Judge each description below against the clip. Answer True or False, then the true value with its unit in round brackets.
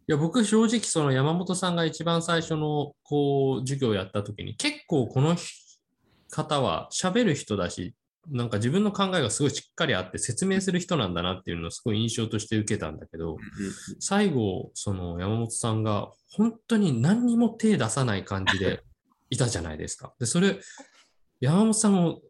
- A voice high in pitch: False (135 Hz)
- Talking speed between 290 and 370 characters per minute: True (340 characters per minute)